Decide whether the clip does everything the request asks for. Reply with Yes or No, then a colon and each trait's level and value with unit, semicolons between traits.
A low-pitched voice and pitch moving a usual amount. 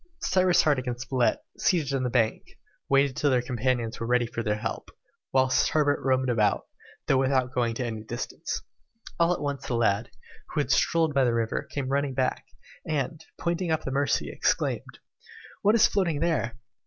Yes: low, 130 Hz; average, 3.6 semitones